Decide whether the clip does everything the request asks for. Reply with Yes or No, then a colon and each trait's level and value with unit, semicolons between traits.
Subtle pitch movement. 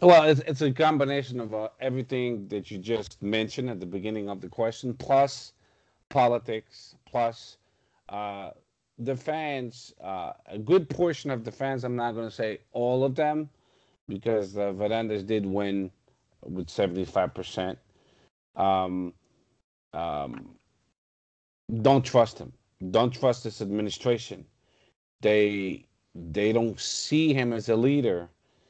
No: average, 4.4 semitones